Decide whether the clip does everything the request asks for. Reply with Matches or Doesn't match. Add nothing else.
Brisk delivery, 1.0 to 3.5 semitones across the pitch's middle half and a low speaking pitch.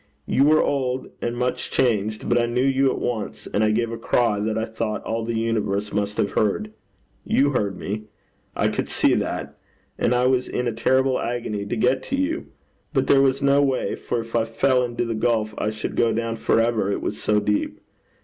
Matches